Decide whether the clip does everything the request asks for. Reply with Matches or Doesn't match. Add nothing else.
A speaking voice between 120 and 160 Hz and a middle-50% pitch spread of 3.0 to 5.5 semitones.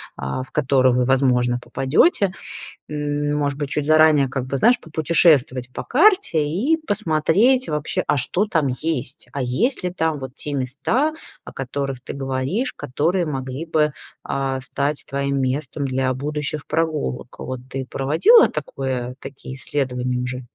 Matches